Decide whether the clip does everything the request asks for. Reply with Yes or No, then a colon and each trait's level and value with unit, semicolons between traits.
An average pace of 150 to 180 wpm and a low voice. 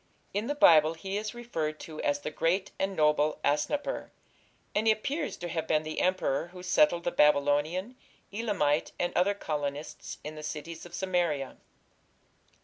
No: average, 160 wpm; medium, 165 Hz